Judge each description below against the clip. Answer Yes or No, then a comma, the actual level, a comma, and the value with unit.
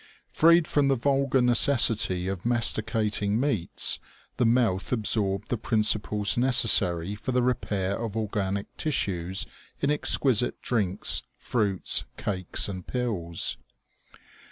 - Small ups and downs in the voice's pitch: No, average, 4.2 semitones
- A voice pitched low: Yes, low, 110 Hz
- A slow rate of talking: Yes, slow, 120 wpm